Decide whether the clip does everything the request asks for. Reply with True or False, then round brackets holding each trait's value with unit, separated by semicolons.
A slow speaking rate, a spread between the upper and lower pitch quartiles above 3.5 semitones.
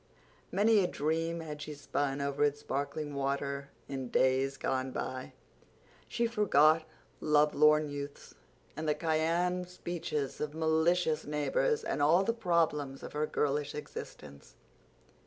False (130 wpm; 2.9 semitones)